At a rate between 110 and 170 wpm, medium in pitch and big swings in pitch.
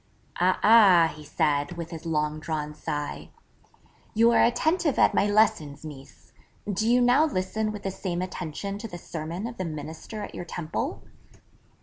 Yes: average, 165 wpm; medium, 180 Hz; wide, 5.7 semitones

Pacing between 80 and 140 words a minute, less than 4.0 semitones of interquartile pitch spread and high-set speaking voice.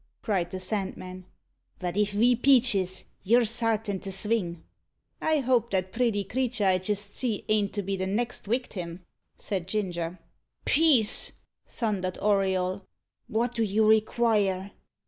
Yes: slow, 135 wpm; average, 3.6 semitones; high, 205 Hz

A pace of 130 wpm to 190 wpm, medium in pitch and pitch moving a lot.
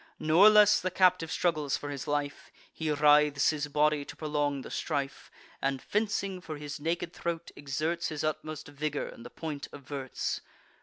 No: average, 165 wpm; medium, 150 Hz; narrow, 2.5 semitones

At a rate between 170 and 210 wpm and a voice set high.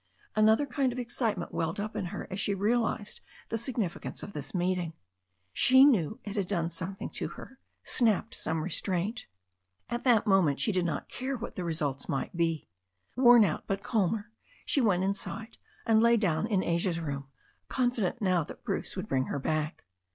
Yes: average, 180 wpm; high, 195 Hz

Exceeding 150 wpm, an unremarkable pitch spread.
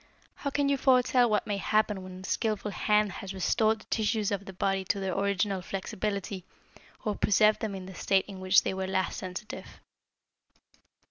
No: average, 185 wpm; narrow, 2.2 semitones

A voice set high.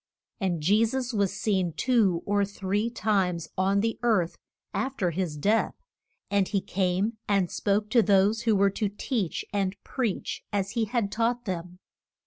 Yes: high, 200 Hz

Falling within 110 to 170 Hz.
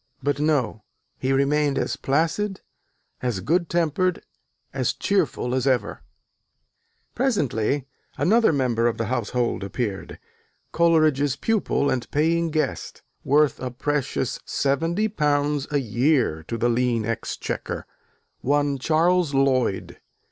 Yes: medium, 140 Hz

